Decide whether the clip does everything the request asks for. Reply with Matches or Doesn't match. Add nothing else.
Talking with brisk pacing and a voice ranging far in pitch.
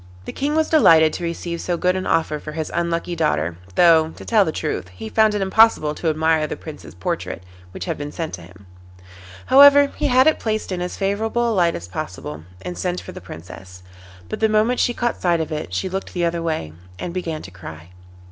Matches